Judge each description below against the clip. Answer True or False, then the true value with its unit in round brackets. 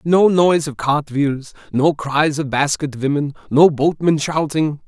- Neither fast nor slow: True (160 wpm)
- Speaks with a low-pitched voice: False (150 Hz)